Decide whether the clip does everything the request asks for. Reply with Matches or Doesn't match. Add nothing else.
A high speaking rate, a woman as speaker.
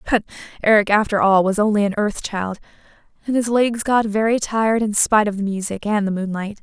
Matches